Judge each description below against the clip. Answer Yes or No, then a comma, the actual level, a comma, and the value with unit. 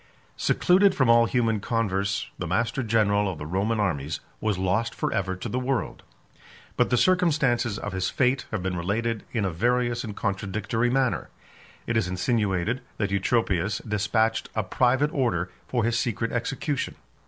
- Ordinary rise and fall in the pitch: Yes, average, 4.0 semitones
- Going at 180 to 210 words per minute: No, average, 165 wpm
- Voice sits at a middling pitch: No, low, 110 Hz